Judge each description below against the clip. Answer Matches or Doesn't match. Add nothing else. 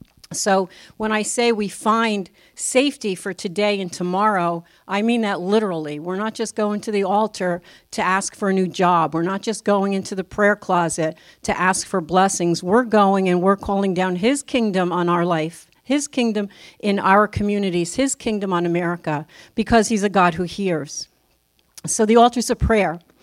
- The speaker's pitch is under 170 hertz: Doesn't match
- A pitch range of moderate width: Matches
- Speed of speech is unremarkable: Matches